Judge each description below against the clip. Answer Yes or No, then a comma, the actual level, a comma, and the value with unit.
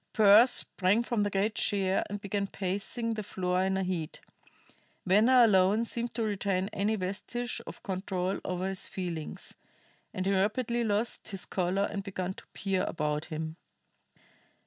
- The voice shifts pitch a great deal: No, average, 2.7 semitones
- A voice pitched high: Yes, high, 195 Hz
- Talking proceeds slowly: No, average, 155 wpm